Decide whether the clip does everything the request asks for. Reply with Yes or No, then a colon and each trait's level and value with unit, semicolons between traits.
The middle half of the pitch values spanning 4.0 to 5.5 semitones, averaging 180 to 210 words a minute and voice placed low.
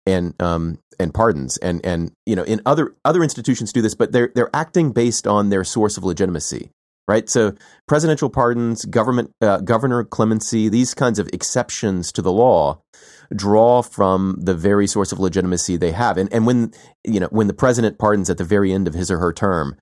Yes: average, 4.4 semitones; average, 200 wpm; low, 105 Hz